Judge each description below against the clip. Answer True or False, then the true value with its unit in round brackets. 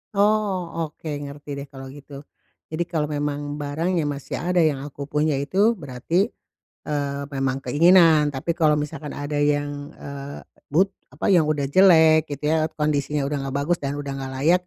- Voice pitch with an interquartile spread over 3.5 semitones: False (2.4 semitones)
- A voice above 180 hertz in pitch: False (150 Hz)